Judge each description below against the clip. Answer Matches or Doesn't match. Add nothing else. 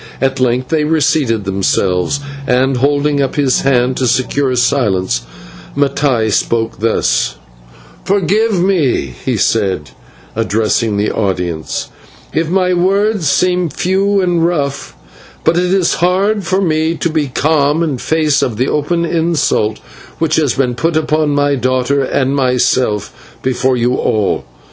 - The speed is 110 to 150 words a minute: Matches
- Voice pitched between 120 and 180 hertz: Matches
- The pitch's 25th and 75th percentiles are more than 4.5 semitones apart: Matches